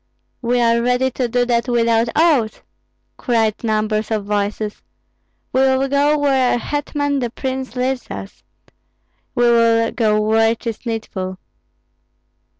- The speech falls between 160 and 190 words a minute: No, slow, 135 wpm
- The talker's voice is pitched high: Yes, high, 235 Hz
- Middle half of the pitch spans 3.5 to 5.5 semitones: No, average, 2.9 semitones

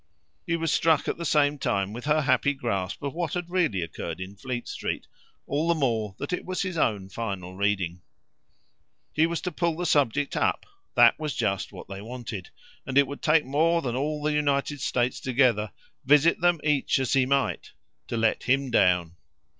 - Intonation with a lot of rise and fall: Yes, wide, 6.3 semitones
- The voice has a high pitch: No, low, 135 Hz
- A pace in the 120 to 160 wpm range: No, average, 195 wpm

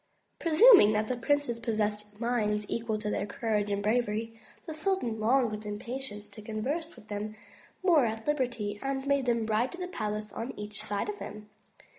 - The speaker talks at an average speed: Yes, average, 180 wpm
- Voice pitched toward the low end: No, high, 225 Hz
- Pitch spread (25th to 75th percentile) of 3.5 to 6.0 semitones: Yes, average, 4.1 semitones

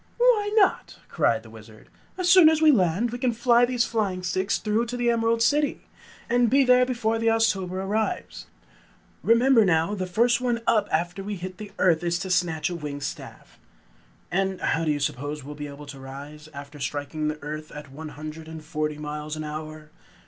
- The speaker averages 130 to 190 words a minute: No, average, 200 wpm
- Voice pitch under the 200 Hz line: Yes, medium, 185 Hz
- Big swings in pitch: Yes, wide, 7.3 semitones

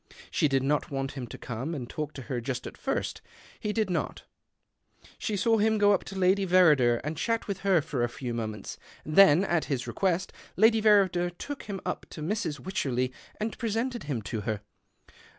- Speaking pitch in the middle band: Yes, medium, 170 Hz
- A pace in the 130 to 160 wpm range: No, average, 195 wpm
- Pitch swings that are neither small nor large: No, wide, 7.4 semitones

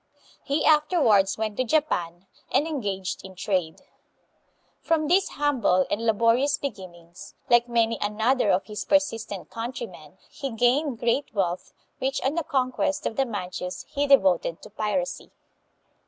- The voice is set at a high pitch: Yes, high, 230 Hz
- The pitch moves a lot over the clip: Yes, wide, 6.4 semitones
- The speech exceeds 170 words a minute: No, average, 140 wpm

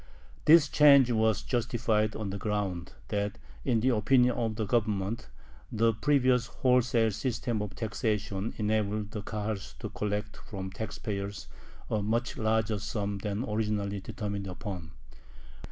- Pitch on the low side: Yes, low, 110 Hz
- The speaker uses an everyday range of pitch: No, narrow, 2.3 semitones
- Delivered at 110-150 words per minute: Yes, average, 140 wpm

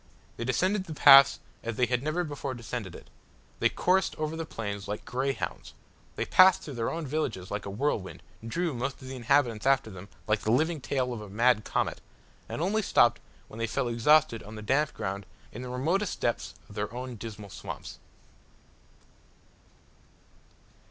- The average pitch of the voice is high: No, low, 125 Hz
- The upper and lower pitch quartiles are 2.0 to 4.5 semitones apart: No, wide, 5.4 semitones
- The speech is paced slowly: No, average, 180 wpm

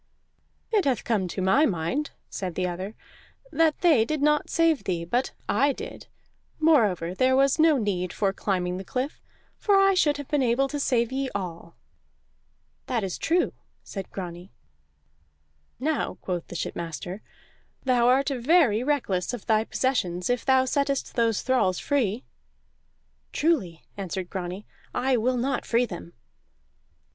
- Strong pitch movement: Yes, wide, 6.9 semitones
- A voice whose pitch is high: Yes, high, 240 Hz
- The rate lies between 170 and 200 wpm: No, average, 150 wpm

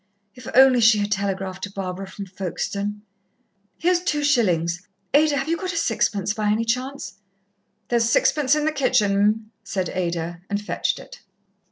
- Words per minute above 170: No, average, 165 wpm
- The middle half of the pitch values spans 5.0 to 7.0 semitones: Yes, wide, 5.6 semitones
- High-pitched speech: Yes, high, 210 Hz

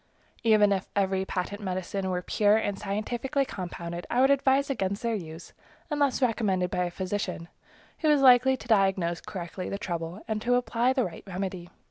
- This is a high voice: Yes, high, 200 Hz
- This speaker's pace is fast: No, average, 175 wpm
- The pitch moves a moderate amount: Yes, average, 4.9 semitones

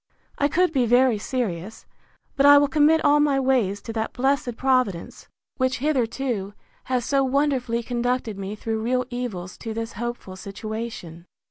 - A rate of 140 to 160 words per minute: Yes, average, 155 wpm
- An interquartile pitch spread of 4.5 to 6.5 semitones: No, average, 3.6 semitones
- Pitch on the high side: Yes, high, 245 Hz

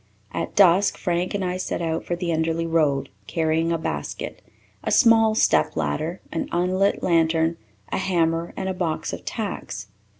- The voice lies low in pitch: No, medium, 170 Hz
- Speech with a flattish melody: Yes, narrow, 2.3 semitones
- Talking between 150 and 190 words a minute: Yes, average, 165 wpm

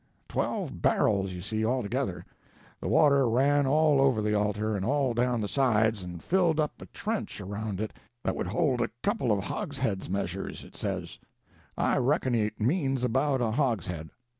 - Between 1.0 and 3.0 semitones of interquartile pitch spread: No, average, 4.9 semitones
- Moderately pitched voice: No, low, 120 Hz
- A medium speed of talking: Yes, average, 170 wpm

